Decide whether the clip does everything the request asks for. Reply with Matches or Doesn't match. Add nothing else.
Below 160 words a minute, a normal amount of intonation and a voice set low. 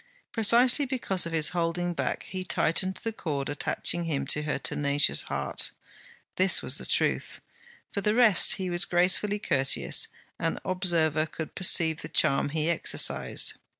Doesn't match